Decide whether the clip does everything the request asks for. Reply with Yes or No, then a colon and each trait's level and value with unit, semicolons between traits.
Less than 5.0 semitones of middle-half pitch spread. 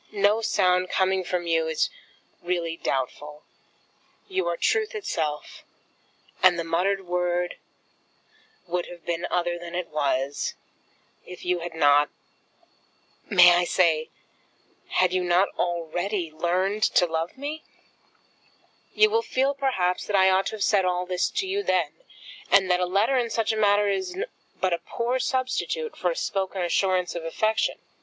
Yes: average, 3.8 semitones